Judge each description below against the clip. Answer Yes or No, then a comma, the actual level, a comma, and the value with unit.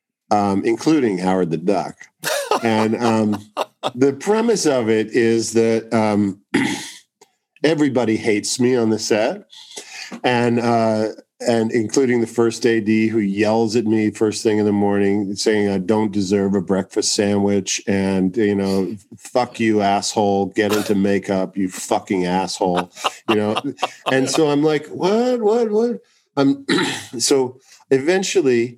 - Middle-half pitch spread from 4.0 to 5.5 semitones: No, average, 3.5 semitones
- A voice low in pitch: Yes, low, 110 Hz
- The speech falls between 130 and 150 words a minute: Yes, average, 140 wpm